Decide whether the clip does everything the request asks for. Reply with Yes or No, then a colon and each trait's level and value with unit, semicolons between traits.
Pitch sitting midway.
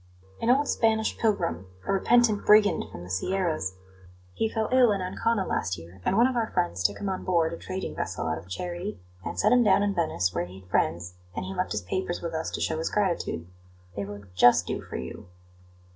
Yes: medium, 175 Hz